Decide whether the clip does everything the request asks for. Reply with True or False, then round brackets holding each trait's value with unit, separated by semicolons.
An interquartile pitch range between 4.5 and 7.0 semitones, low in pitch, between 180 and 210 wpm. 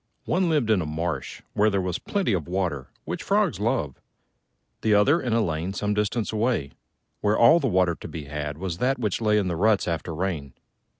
True (5.2 semitones; 95 Hz; 205 wpm)